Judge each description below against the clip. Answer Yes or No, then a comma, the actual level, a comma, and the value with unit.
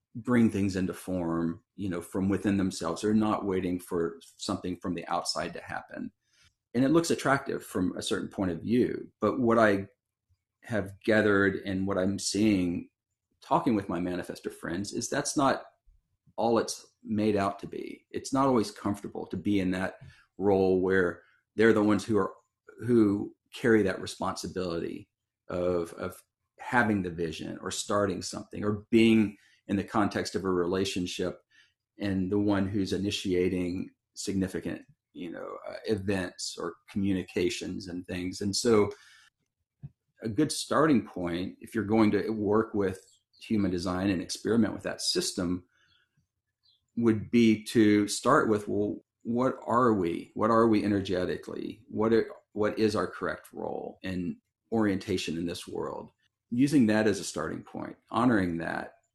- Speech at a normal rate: Yes, average, 155 wpm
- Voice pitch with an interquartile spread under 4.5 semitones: Yes, average, 2.8 semitones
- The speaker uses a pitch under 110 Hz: Yes, low, 100 Hz